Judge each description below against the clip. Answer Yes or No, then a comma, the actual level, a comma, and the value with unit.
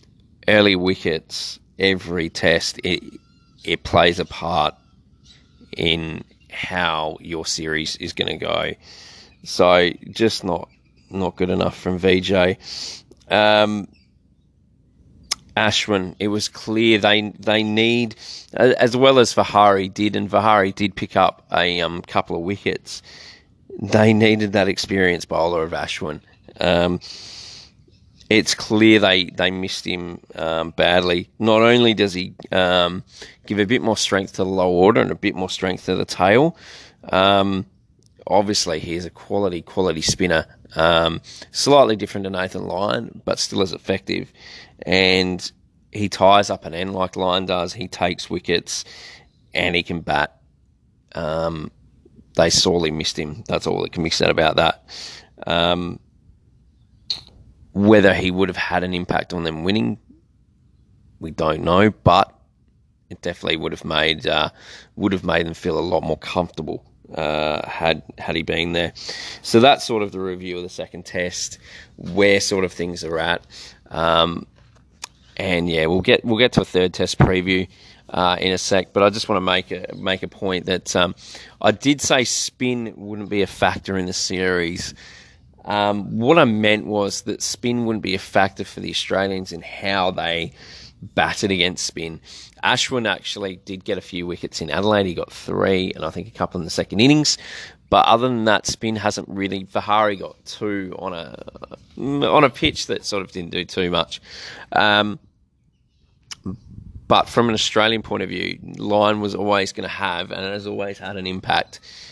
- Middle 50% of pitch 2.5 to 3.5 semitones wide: Yes, average, 2.9 semitones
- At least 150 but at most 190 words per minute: Yes, average, 165 wpm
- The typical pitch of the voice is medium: No, very low, 95 Hz